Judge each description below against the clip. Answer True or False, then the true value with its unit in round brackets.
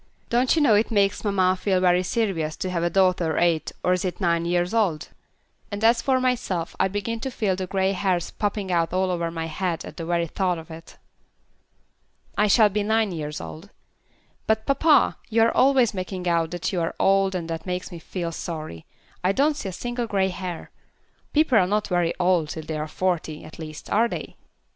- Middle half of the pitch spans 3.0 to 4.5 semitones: True (3.8 semitones)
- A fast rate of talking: True (210 wpm)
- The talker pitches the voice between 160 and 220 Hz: True (185 Hz)